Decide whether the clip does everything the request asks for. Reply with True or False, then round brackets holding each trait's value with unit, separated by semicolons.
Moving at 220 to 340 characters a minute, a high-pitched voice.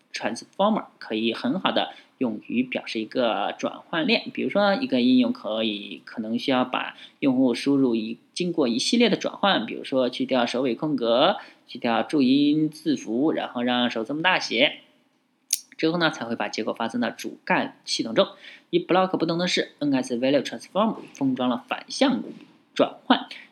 False (320 characters per minute; 165 Hz)